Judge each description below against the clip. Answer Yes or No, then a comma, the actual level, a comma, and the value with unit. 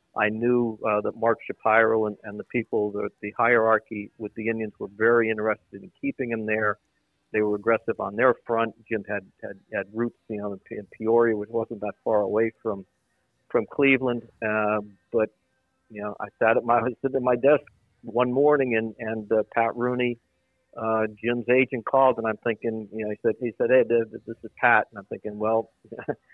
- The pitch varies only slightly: Yes, narrow, 1.9 semitones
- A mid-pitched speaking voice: No, low, 110 Hz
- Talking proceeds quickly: No, average, 195 wpm